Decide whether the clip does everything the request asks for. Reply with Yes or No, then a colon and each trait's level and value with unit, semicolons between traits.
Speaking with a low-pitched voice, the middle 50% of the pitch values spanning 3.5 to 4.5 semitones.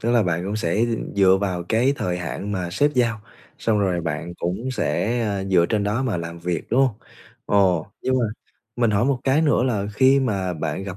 No: low, 100 Hz; average, 5.1 semitones